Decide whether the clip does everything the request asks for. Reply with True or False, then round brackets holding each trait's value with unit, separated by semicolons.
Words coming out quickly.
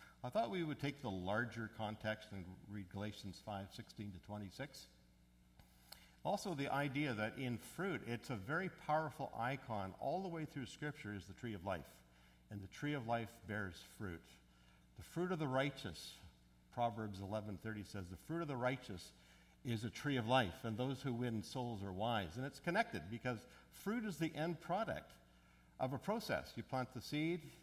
False (185 wpm)